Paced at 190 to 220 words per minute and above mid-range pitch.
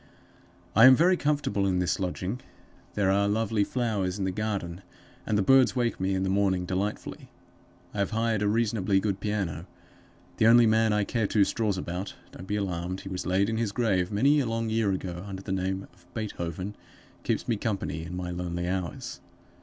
No: average, 195 wpm; low, 100 Hz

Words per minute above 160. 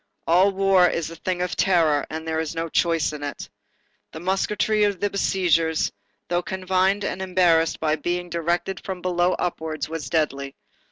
Yes: average, 170 wpm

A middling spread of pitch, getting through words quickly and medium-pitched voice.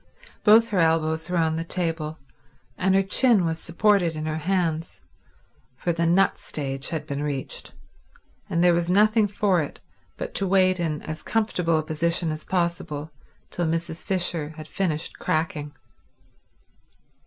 No: average, 3.0 semitones; average, 155 wpm; medium, 170 Hz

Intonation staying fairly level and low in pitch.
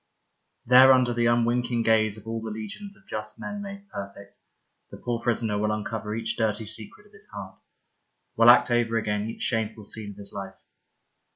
Yes: narrow, 2.2 semitones; low, 110 Hz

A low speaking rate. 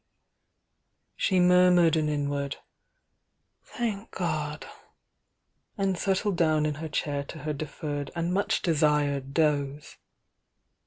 Yes: slow, 115 wpm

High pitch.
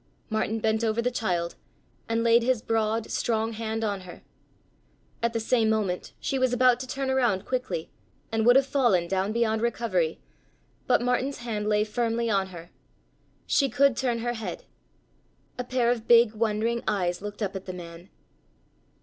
Yes: high, 225 Hz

